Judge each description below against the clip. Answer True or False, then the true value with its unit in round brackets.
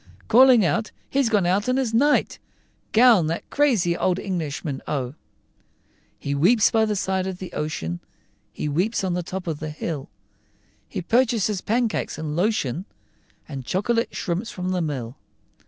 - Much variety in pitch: True (6.3 semitones)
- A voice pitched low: False (185 Hz)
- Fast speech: False (155 wpm)